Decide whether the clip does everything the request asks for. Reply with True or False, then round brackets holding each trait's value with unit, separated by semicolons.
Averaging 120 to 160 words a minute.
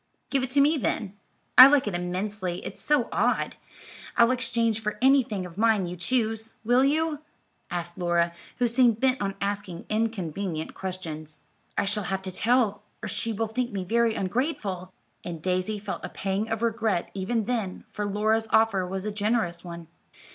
False (175 wpm)